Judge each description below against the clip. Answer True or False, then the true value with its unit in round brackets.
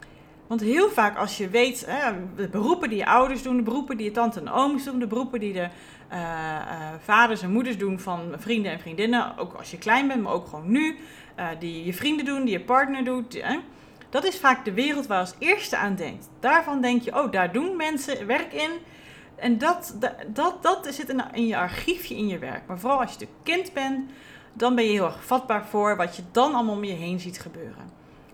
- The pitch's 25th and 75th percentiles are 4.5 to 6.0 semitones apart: True (5.4 semitones)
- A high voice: True (235 Hz)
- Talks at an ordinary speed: False (220 wpm)